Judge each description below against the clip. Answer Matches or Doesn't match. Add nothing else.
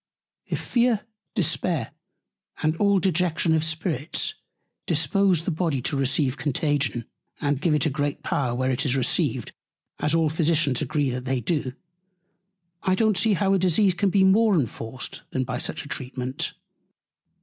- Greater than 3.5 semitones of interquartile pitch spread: Matches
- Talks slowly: Doesn't match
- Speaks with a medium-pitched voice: Matches